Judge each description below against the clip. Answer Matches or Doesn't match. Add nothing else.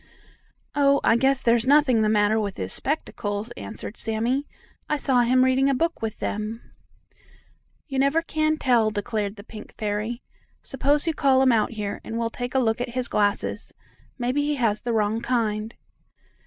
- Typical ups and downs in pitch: Matches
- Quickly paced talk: Doesn't match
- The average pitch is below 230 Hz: Doesn't match